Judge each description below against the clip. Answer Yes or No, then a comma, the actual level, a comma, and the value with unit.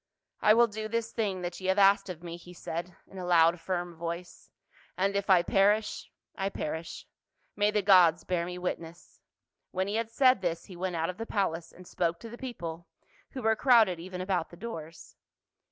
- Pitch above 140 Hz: Yes, medium, 185 Hz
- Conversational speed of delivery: No, fast, 215 wpm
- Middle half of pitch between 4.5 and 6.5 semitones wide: No, average, 3.3 semitones